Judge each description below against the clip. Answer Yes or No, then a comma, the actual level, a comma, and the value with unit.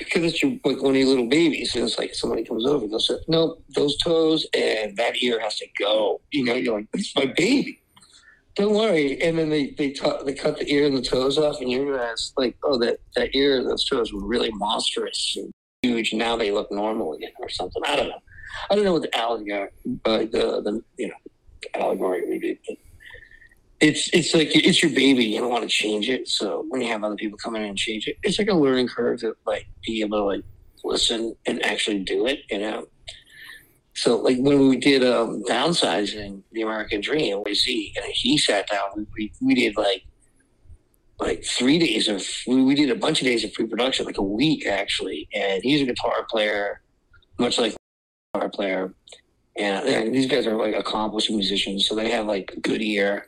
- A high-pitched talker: No, low, 135 Hz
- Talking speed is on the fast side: Yes, fast, 215 wpm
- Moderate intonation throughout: No, wide, 8.1 semitones